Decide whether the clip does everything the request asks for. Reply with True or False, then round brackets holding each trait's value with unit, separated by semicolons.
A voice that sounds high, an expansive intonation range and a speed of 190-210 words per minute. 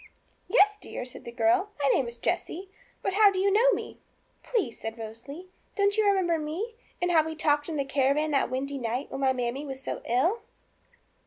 True (305 Hz; 6.6 semitones; 200 wpm)